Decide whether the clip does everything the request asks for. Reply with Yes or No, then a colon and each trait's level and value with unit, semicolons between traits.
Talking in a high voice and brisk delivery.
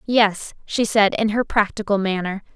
No: high, 210 Hz; average, 165 wpm